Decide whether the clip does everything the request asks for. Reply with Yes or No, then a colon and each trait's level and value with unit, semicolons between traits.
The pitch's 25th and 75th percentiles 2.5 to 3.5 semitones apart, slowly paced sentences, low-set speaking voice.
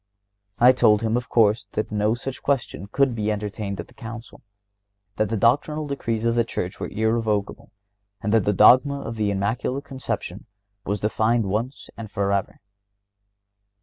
No: average, 2.8 semitones; average, 160 wpm; low, 110 Hz